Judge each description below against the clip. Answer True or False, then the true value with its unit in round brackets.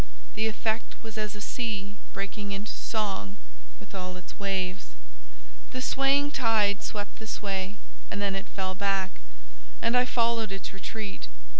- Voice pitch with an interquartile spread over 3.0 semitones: False (2.4 semitones)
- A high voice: True (205 Hz)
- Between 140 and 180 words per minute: True (150 wpm)